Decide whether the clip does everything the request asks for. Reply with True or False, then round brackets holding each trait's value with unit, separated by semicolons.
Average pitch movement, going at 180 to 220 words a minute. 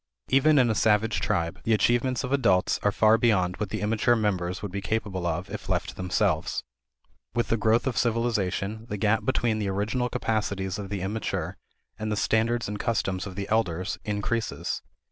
True (3.0 semitones; 185 wpm)